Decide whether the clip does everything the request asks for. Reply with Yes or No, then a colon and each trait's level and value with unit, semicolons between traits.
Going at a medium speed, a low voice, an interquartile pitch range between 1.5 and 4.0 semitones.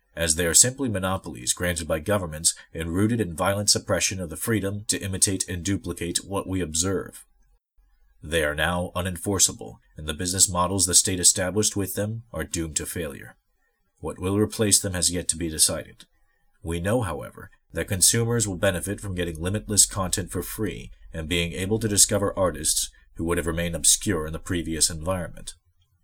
Yes: average, 175 wpm; very low, 90 Hz; average, 2.8 semitones